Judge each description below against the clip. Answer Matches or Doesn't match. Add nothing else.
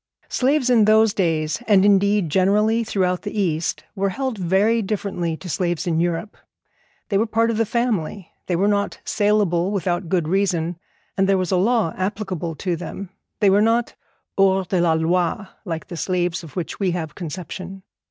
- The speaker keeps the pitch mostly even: Doesn't match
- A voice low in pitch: Doesn't match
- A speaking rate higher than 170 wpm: Matches